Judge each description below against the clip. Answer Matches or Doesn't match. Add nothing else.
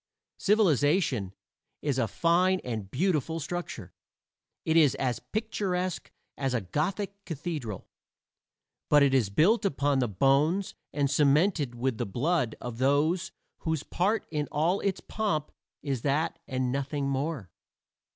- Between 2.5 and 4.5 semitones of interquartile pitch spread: Doesn't match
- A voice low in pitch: Doesn't match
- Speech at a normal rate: Doesn't match